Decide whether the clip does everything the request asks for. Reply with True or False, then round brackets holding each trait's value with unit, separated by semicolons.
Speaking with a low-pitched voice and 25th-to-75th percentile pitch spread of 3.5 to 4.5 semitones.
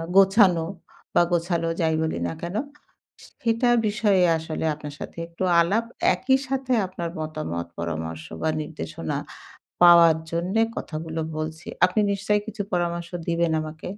False (170 Hz; 3.8 semitones)